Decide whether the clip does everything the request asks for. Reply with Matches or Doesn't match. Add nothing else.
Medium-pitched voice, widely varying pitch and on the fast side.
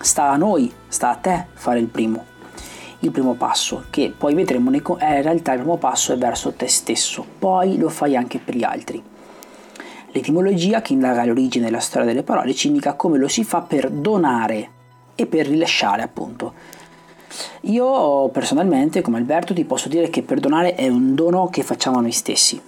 Matches